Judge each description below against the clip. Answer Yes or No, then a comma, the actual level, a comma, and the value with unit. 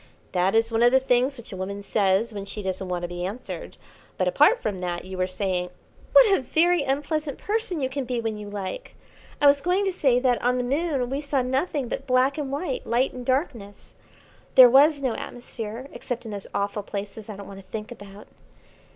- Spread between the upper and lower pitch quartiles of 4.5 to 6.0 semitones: Yes, wide, 5.5 semitones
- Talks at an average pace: No, fast, 220 wpm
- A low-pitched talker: No, high, 245 Hz